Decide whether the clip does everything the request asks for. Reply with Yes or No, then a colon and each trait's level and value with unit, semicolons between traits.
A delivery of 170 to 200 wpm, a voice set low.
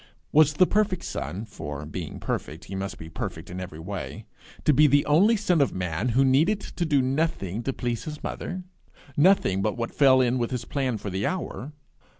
Yes: average, 190 wpm; low, 130 Hz